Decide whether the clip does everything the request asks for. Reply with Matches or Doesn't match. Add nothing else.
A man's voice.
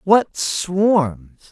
Matches